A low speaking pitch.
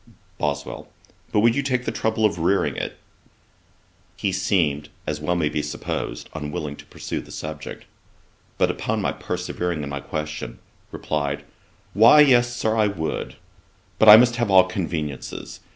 Yes: very low, 90 Hz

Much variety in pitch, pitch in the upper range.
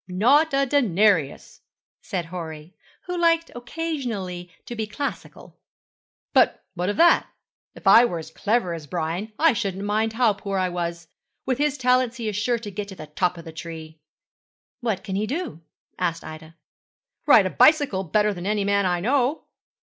Yes: wide, 5.8 semitones; high, 205 Hz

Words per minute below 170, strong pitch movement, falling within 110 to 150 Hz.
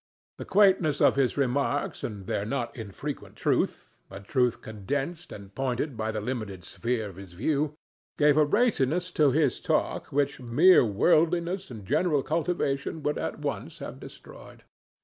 Yes: average, 150 wpm; wide, 5.8 semitones; medium, 140 Hz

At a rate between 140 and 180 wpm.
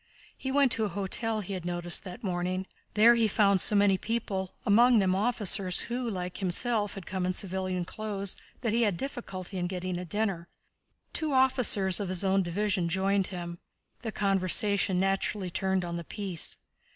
Yes: average, 175 wpm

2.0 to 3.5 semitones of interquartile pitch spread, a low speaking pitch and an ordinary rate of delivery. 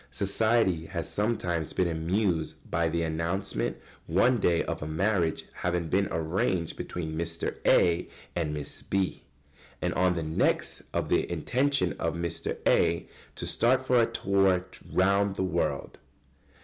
Yes: average, 3.1 semitones; very low, 90 Hz; average, 150 wpm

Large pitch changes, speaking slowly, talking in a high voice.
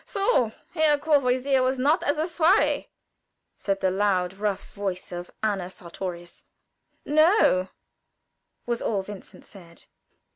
Yes: wide, 7.8 semitones; slow, 120 wpm; high, 215 Hz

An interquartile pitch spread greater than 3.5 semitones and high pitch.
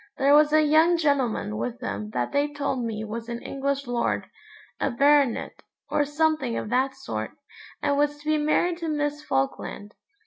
Yes: average, 4.2 semitones; very high, 280 Hz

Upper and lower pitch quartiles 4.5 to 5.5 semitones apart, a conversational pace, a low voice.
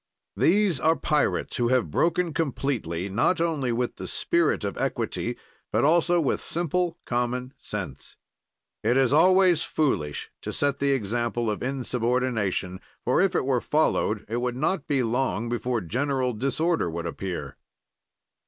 Yes: average, 5.1 semitones; average, 145 wpm; low, 130 Hz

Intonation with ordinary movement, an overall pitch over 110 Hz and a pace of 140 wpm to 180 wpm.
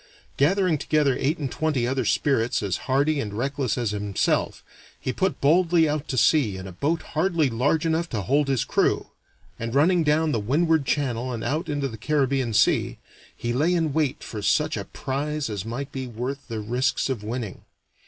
No: average, 4.5 semitones; medium, 140 Hz; average, 190 wpm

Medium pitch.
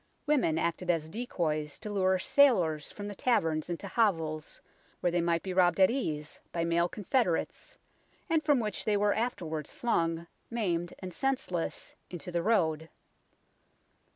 Yes: medium, 175 Hz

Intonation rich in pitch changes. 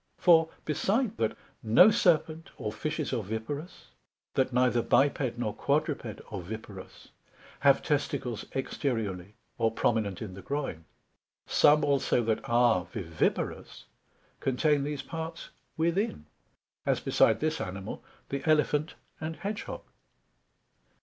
Yes: wide, 5.9 semitones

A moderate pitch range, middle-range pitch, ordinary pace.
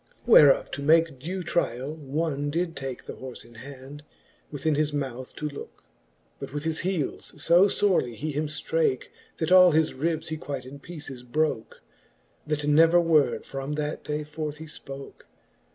Yes: average, 3.0 semitones; medium, 150 Hz; average, 170 wpm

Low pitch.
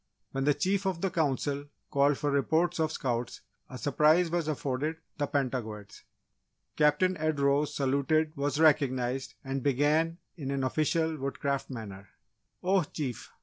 No: medium, 145 Hz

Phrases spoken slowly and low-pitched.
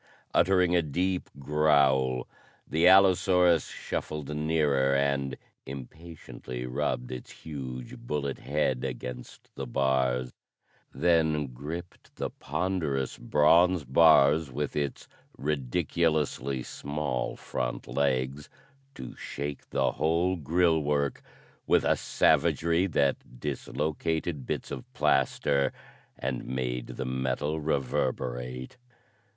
Yes: slow, 100 wpm; very low, 70 Hz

